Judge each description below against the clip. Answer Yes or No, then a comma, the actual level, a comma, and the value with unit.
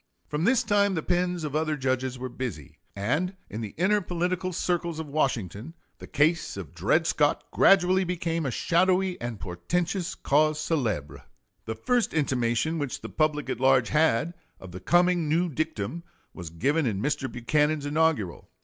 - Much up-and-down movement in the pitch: Yes, wide, 6.2 semitones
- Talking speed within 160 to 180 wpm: Yes, average, 165 wpm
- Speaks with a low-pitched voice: No, medium, 155 Hz